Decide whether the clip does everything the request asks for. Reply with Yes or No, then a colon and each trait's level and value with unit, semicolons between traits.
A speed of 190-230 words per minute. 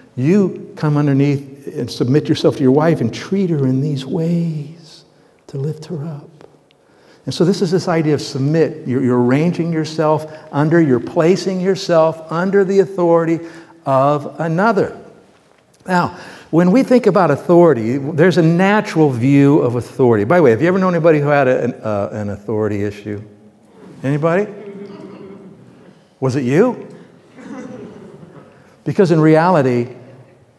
No: average, 145 wpm